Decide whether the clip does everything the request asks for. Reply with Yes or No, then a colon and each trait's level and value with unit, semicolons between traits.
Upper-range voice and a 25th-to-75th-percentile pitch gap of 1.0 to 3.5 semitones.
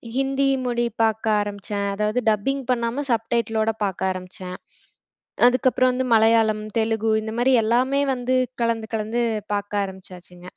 Yes: high, 225 Hz; average, 3.1 semitones